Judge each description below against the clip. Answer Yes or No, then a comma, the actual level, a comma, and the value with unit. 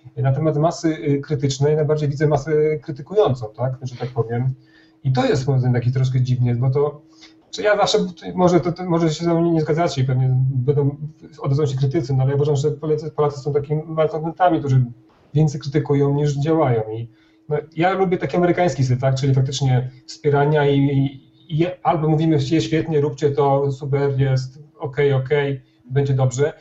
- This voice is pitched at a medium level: Yes, medium, 145 Hz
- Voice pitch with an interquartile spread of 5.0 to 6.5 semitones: No, average, 2.8 semitones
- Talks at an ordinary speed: No, fast, 170 wpm